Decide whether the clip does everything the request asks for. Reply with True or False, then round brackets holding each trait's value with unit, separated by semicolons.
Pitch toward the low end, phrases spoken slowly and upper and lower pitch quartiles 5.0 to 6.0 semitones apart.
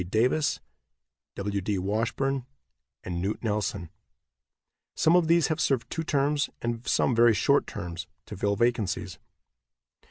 True (115 Hz; 130 wpm; 5.6 semitones)